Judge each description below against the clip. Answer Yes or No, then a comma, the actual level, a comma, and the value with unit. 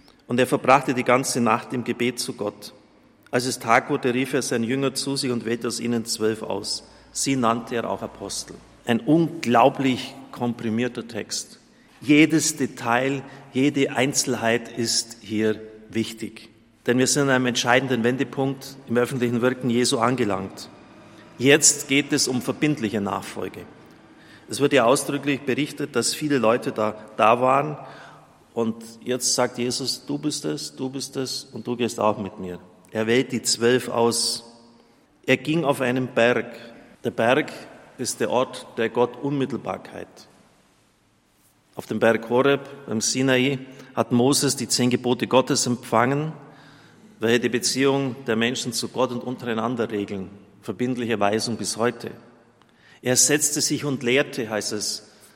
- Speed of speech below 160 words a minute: Yes, average, 150 wpm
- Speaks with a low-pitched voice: Yes, low, 125 Hz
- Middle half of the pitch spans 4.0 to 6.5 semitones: No, average, 2.8 semitones